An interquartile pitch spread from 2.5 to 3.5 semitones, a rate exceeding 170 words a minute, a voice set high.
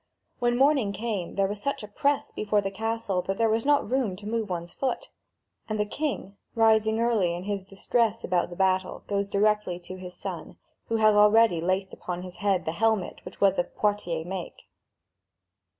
Yes: average, 3.2 semitones; average, 190 wpm; high, 205 Hz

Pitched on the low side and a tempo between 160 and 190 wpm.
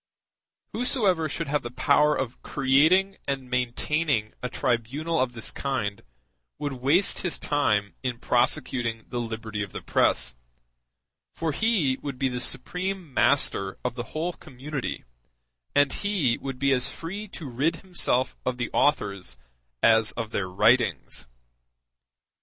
No: low, 130 Hz; average, 140 wpm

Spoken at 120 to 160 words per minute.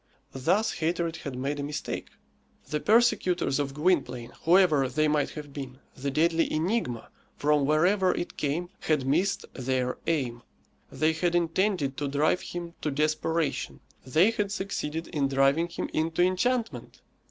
Yes: average, 145 wpm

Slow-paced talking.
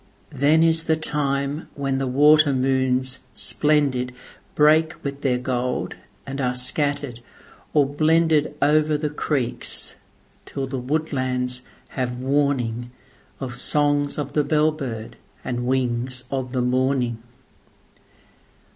Yes: slow, 110 wpm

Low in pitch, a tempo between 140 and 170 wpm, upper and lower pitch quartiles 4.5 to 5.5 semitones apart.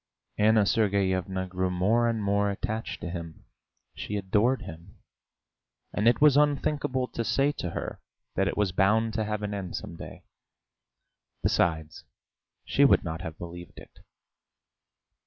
No: low, 100 Hz; average, 145 wpm; average, 3.7 semitones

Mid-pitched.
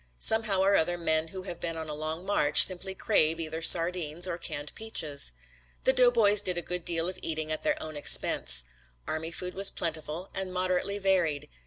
Yes: medium, 170 Hz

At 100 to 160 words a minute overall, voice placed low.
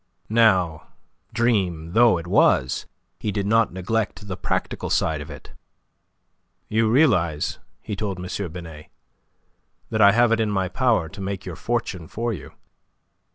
Yes: average, 150 wpm; low, 100 Hz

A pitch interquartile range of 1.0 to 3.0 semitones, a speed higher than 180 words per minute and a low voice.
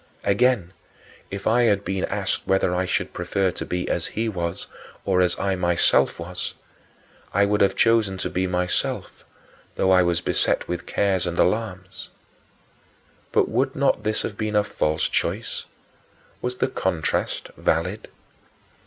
No: average, 2.7 semitones; average, 155 wpm; very low, 95 Hz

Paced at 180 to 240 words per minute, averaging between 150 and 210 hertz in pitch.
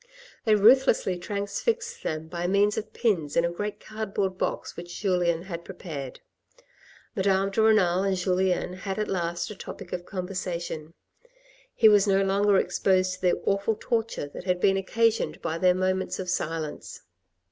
No: average, 160 wpm; high, 190 Hz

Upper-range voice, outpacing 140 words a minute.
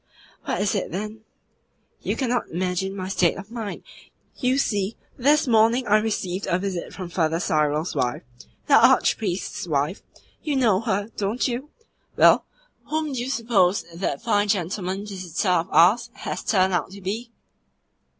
Yes: high, 200 Hz; average, 155 wpm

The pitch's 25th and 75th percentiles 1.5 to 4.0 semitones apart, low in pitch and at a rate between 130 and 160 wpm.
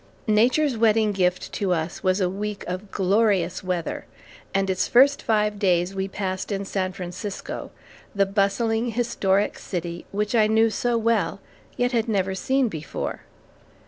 No: average, 3.1 semitones; high, 200 Hz; average, 150 wpm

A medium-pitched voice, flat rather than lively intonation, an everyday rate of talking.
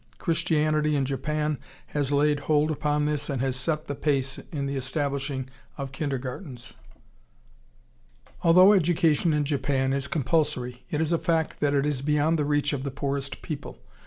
Yes: medium, 145 Hz; narrow, 1.9 semitones; average, 160 wpm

